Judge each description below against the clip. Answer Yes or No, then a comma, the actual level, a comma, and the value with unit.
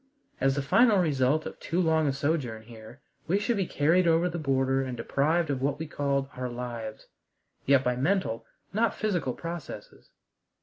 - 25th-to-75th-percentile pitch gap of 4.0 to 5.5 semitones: Yes, average, 4.7 semitones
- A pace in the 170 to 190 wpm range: Yes, average, 175 wpm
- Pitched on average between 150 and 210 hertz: No, medium, 140 Hz